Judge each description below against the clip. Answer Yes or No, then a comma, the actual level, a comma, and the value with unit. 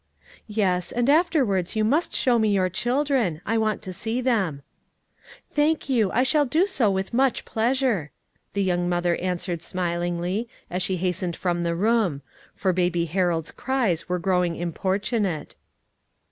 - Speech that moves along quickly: No, average, 150 wpm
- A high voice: Yes, high, 195 Hz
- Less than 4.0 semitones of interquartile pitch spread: No, wide, 5.4 semitones